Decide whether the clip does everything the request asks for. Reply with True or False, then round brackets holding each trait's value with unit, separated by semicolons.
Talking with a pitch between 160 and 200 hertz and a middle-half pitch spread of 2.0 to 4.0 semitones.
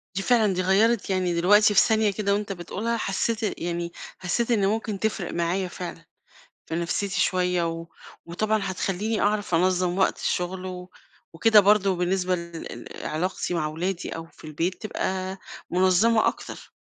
True (185 Hz; 2.9 semitones)